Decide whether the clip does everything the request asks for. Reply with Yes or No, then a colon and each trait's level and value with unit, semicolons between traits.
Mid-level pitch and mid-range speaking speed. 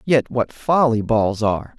No: low, 120 Hz; average, 170 wpm